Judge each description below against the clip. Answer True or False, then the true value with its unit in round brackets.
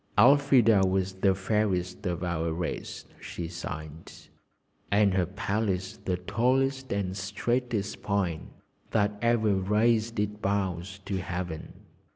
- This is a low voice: True (100 Hz)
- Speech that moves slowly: True (120 wpm)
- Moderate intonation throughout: True (3.2 semitones)